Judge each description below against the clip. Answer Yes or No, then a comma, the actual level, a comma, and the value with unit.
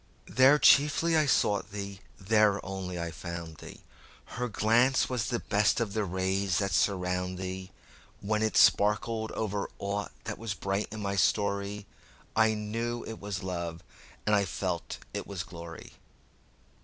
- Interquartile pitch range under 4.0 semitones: Yes, average, 2.8 semitones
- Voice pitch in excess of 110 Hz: No, low, 100 Hz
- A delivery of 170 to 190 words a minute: No, average, 145 wpm